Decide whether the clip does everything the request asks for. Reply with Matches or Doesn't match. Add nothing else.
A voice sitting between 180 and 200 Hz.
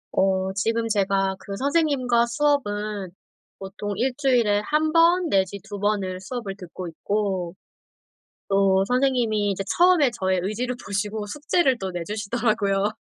Doesn't match